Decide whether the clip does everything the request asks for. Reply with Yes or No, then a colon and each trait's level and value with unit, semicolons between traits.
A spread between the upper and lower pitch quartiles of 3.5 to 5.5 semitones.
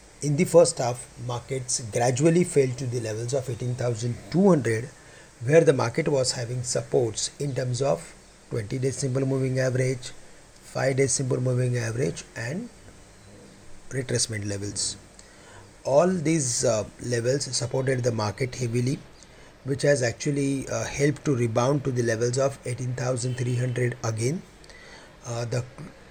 No: average, 2.7 semitones